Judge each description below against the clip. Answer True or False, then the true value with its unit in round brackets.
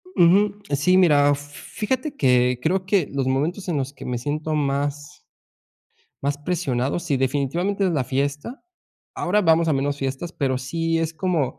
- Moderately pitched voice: True (145 Hz)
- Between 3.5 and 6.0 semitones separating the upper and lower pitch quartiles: True (4.2 semitones)